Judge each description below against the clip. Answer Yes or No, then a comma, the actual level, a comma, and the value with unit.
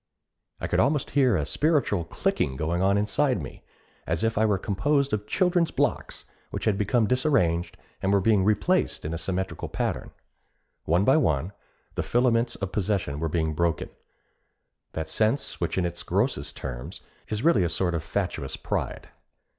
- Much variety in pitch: Yes, wide, 6.3 semitones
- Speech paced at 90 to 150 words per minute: No, average, 170 wpm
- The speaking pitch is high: No, low, 100 Hz